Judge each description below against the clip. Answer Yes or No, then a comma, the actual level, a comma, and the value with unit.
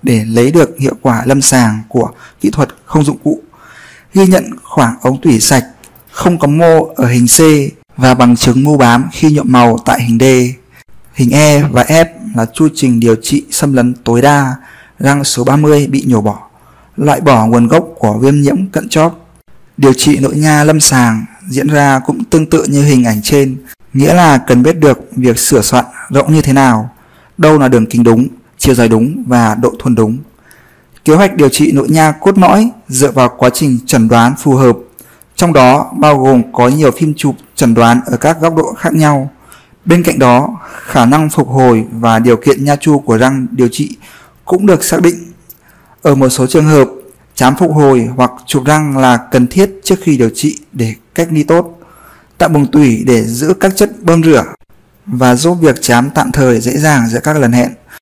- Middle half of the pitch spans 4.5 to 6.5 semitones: No, average, 4.0 semitones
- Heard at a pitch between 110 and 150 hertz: Yes, low, 135 Hz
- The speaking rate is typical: Yes, average, 205 wpm